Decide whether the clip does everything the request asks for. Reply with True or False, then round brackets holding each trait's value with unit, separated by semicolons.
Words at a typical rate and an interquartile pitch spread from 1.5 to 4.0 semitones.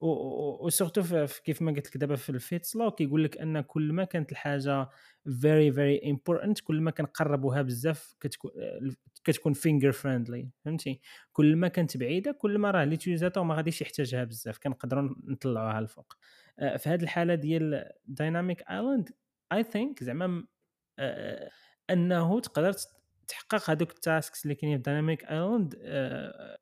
False (145 wpm; 3.6 semitones)